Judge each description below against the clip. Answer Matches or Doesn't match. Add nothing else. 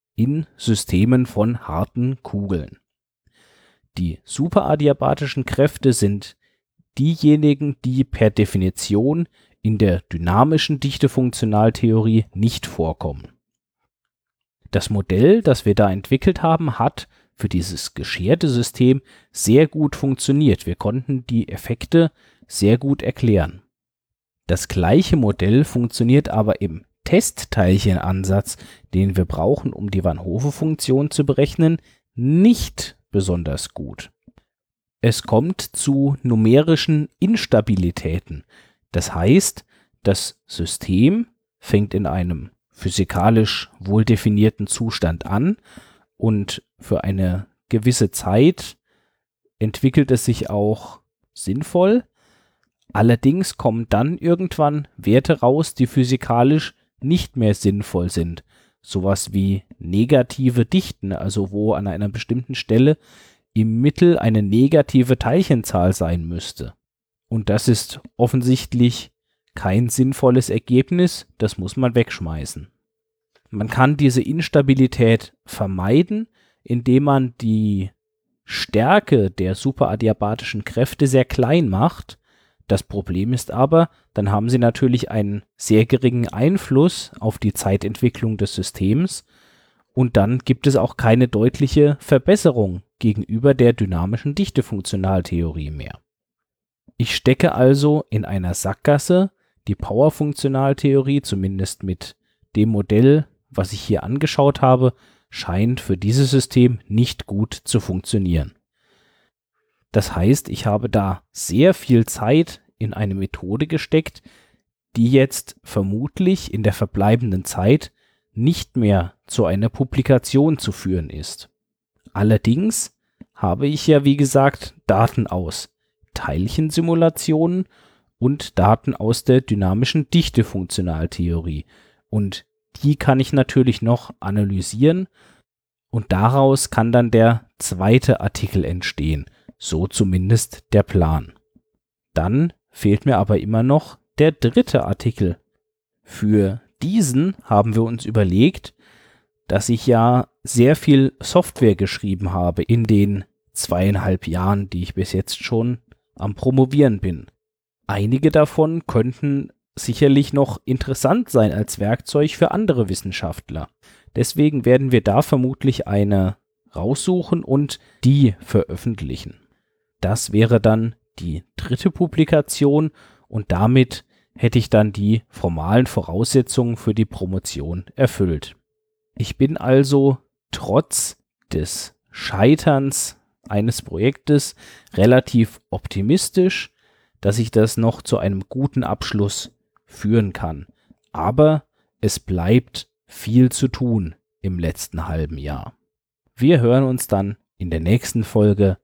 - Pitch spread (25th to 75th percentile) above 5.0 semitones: Matches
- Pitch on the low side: Matches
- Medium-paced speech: Doesn't match